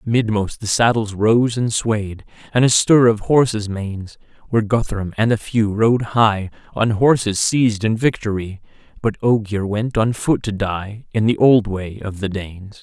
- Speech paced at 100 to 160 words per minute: No, average, 180 wpm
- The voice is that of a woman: No, male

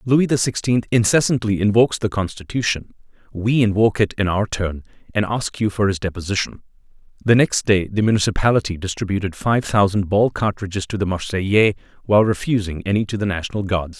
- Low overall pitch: Yes, low, 105 Hz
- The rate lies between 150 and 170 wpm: Yes, average, 165 wpm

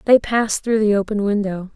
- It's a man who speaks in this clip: No, female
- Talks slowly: No, fast, 205 wpm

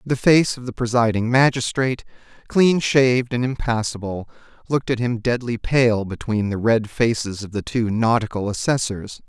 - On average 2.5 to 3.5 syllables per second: No, 4.9 syllables/s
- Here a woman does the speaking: No, male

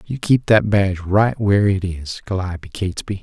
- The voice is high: No, low, 100 Hz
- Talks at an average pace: Yes, average, 185 wpm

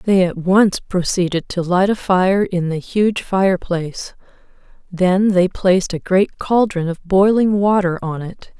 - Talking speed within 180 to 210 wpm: No, average, 160 wpm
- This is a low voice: No, medium, 185 Hz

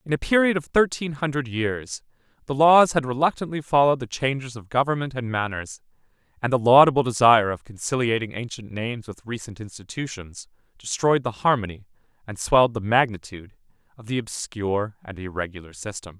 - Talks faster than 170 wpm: No, average, 155 wpm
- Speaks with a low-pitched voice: Yes, low, 120 Hz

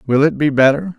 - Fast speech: Yes, fast, 245 wpm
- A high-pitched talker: No, medium, 145 Hz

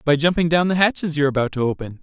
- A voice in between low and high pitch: Yes, medium, 155 Hz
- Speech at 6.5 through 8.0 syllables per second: Yes, 7.3 syllables/s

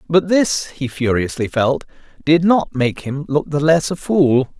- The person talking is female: No, male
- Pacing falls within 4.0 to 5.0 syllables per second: Yes, 4.1 syllables/s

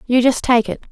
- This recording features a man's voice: No, female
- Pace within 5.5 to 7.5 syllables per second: Yes, 5.8 syllables/s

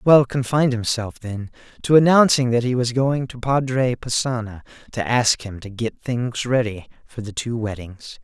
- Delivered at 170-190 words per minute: Yes, average, 175 wpm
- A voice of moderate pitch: No, low, 120 Hz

